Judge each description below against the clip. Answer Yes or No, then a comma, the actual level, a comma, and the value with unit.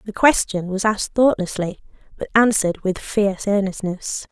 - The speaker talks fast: No, average, 140 wpm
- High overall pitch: Yes, high, 200 Hz